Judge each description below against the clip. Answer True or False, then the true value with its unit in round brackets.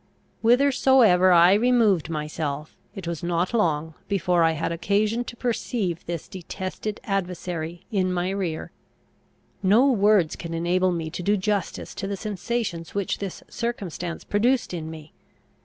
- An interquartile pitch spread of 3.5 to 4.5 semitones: True (4.0 semitones)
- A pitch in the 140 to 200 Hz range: True (185 Hz)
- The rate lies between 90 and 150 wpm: True (140 wpm)